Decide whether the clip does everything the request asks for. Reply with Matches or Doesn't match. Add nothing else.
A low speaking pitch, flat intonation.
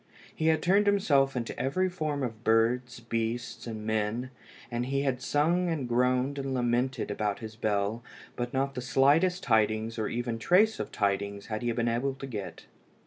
Doesn't match